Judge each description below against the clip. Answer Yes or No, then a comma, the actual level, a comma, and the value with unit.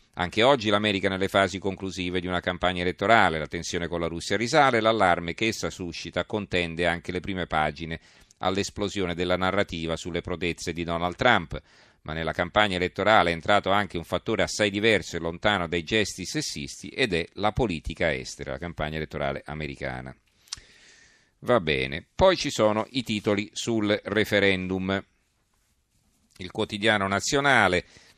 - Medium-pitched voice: No, very low, 90 Hz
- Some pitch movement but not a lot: Yes, average, 3.6 semitones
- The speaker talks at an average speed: Yes, average, 150 wpm